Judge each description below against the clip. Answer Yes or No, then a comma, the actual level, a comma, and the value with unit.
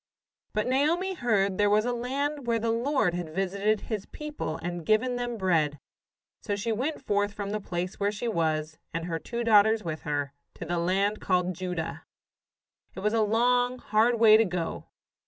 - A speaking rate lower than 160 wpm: No, average, 190 wpm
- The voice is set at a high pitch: Yes, high, 210 Hz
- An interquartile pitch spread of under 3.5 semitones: No, average, 4.9 semitones